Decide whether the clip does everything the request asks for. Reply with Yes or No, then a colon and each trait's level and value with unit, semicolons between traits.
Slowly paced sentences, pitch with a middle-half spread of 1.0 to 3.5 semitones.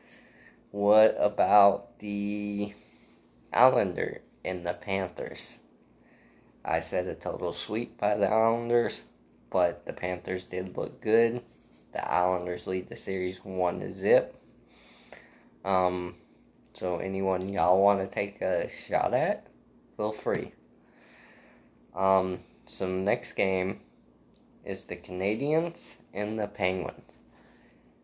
Yes: slow, 110 wpm; narrow, 2.4 semitones